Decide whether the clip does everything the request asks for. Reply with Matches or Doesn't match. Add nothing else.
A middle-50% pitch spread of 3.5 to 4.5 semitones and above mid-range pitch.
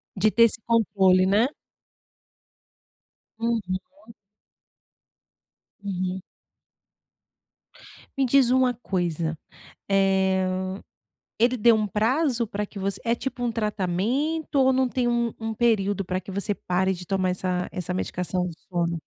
Matches